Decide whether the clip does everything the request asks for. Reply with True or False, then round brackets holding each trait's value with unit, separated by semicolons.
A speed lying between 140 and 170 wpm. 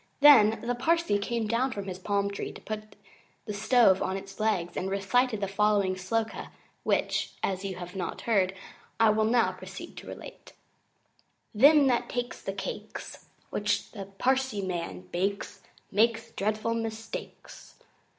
True (150 wpm)